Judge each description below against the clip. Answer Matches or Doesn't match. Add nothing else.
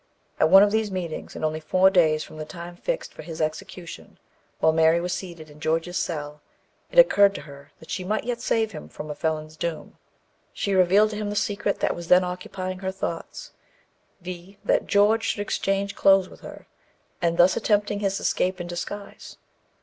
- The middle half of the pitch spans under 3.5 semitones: Doesn't match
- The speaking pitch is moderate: Matches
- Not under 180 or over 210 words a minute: Matches